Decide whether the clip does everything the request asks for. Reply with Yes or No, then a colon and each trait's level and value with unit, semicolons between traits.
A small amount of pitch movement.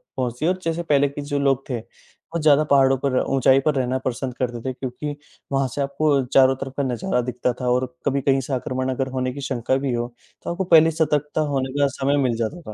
Yes: narrow, 2.1 semitones